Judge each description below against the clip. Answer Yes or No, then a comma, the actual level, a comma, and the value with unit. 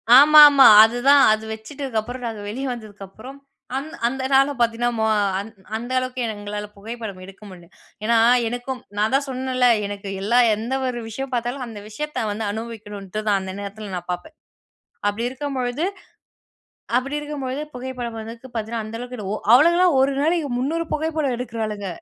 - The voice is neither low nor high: No, high, 240 Hz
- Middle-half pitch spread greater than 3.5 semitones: Yes, average, 3.9 semitones